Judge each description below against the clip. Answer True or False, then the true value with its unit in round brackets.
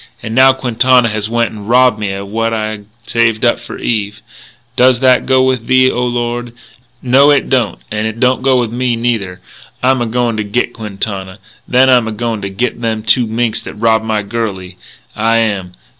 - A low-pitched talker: True (115 Hz)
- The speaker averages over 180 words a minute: True (200 wpm)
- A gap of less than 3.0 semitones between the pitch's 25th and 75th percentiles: True (2.5 semitones)